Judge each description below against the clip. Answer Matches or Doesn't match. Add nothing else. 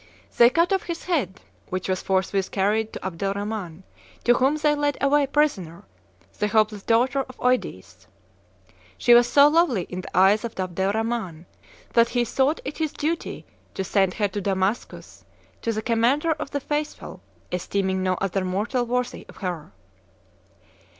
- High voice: Matches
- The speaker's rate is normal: Matches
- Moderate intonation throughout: Doesn't match